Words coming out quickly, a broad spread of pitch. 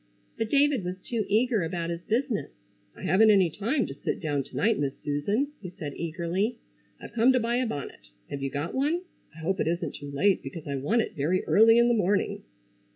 Yes: fast, 220 wpm; wide, 6.4 semitones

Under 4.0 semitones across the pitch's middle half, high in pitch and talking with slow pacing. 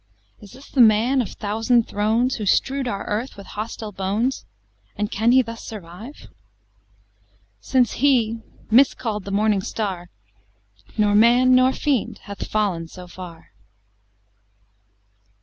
Yes: average, 3.5 semitones; high, 220 Hz; slow, 130 wpm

